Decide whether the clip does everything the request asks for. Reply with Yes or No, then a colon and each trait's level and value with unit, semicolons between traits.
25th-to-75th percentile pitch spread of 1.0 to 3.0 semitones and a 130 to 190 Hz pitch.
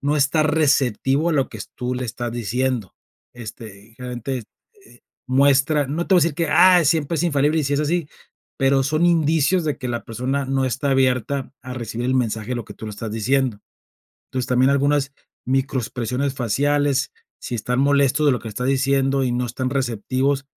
Yes: narrow, 2.6 semitones; low, 135 Hz